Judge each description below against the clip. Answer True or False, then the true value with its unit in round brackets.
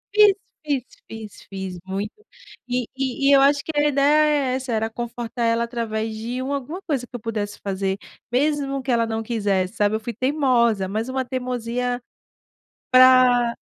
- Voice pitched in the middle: False (245 Hz)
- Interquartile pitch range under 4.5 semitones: True (3.4 semitones)